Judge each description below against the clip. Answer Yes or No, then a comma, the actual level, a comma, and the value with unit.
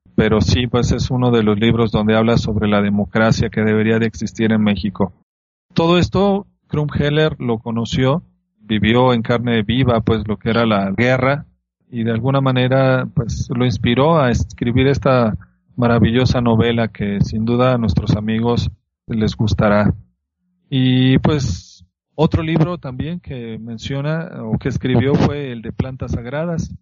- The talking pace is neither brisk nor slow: Yes, average, 155 wpm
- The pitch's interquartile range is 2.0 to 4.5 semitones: Yes, average, 3.6 semitones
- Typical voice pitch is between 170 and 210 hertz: No, low, 120 Hz